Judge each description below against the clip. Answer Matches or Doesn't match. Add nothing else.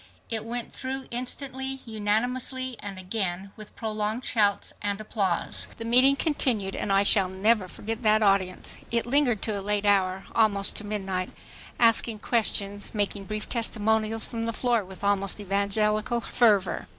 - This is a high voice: Matches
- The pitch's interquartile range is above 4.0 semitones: Doesn't match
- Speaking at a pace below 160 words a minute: Matches